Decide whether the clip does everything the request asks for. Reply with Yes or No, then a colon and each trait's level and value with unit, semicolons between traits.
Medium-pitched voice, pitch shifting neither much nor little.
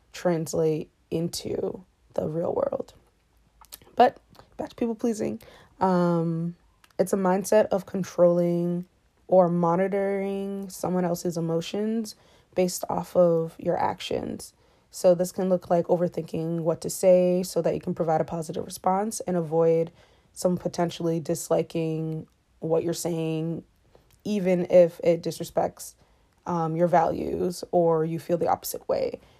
No: medium, 175 Hz; narrow, 2.0 semitones